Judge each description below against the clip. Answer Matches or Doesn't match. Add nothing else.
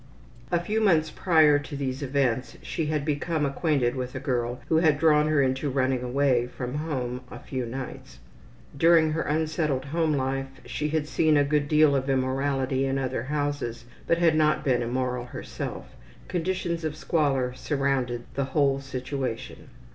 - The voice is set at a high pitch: Doesn't match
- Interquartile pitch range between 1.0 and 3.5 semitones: Matches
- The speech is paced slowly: Doesn't match